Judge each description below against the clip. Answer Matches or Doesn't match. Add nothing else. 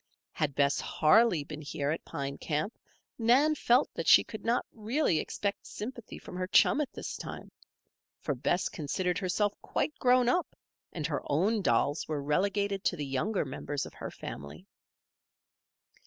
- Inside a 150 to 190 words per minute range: Matches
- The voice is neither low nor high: Matches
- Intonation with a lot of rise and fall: Matches